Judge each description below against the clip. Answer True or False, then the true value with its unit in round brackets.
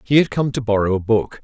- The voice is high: False (115 Hz)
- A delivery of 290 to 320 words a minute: True (295 wpm)